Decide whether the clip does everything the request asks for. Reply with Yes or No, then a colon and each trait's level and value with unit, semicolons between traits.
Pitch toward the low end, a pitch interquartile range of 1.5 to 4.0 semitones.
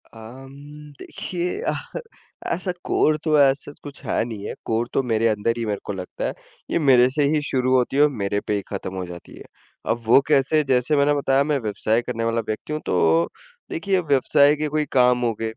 No: low, 130 Hz; average, 4.7 semitones